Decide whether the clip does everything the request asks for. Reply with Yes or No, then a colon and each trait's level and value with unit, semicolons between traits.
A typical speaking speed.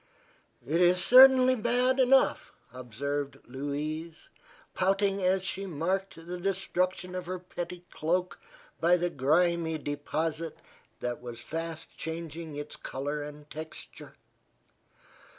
No: slow, 115 wpm